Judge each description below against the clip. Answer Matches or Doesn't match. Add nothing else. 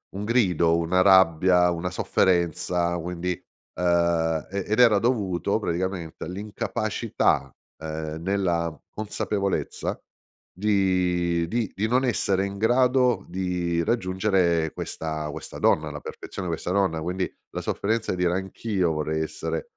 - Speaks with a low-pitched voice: Matches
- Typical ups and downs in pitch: Matches